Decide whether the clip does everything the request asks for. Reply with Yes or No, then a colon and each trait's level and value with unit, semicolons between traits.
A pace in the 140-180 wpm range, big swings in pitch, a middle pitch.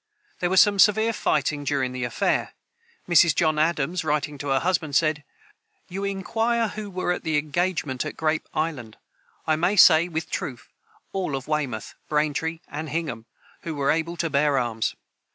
No: average, 170 wpm; average, 3.6 semitones; medium, 155 Hz